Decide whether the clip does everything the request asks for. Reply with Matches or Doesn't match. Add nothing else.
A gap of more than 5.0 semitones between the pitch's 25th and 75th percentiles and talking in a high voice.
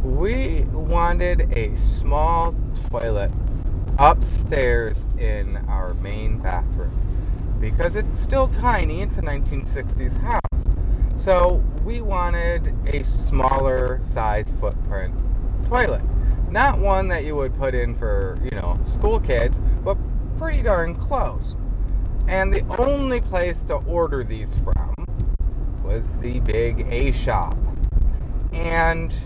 Doesn't match